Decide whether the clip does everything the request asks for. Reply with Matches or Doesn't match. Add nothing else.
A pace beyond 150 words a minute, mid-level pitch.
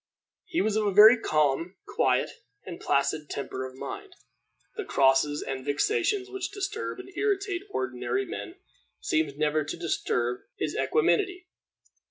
Doesn't match